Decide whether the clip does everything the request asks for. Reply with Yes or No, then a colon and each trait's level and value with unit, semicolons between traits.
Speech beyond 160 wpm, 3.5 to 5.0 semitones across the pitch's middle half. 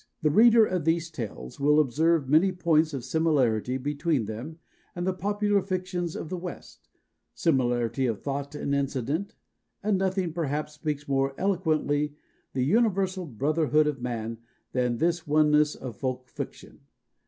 No: average, 145 wpm; average, 4.7 semitones